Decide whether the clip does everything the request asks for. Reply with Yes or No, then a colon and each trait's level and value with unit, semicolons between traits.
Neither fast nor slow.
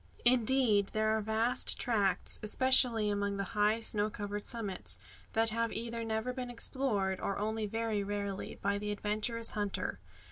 Yes: average, 150 wpm